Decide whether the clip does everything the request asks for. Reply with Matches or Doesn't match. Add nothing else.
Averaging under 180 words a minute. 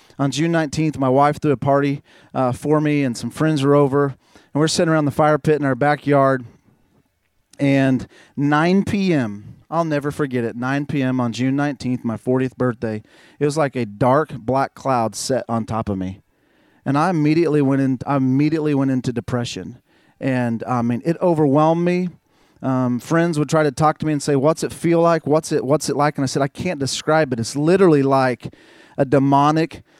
Doesn't match